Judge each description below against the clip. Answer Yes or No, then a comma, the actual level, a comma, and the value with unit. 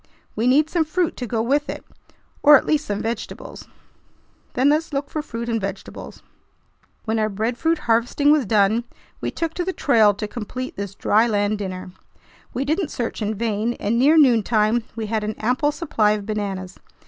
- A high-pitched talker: Yes, high, 230 Hz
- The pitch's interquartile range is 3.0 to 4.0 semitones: No, average, 5.2 semitones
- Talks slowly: No, average, 185 wpm